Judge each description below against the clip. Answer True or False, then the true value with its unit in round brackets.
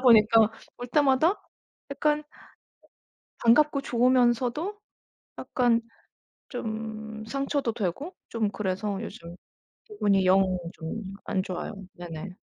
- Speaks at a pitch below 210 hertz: False (230 Hz)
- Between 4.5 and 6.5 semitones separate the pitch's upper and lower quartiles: True (5.2 semitones)